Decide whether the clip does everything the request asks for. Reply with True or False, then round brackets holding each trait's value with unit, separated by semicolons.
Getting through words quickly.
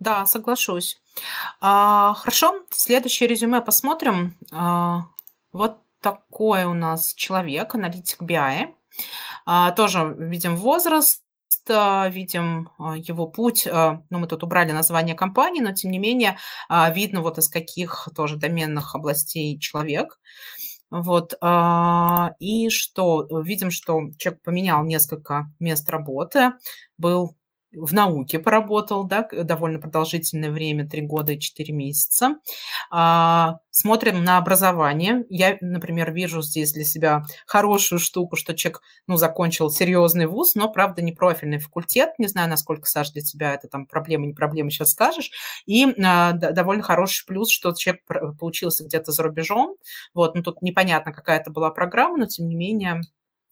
False (130 wpm)